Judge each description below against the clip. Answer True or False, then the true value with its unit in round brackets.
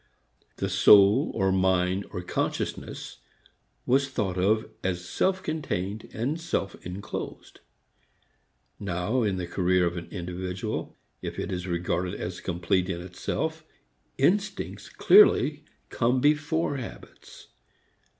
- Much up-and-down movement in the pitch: True (6.6 semitones)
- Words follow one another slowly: True (115 wpm)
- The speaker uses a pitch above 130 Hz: False (95 Hz)